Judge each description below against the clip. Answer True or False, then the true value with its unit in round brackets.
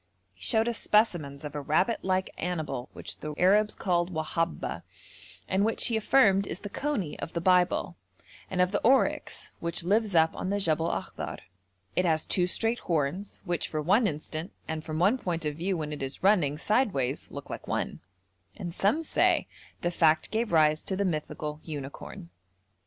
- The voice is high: False (175 Hz)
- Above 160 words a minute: True (180 wpm)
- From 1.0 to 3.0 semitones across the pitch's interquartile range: False (4.5 semitones)